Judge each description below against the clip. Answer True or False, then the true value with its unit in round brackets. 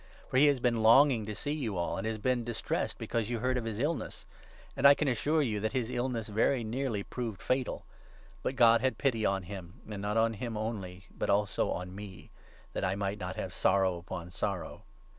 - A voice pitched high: False (110 Hz)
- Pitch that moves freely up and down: False (4.1 semitones)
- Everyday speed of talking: False (220 wpm)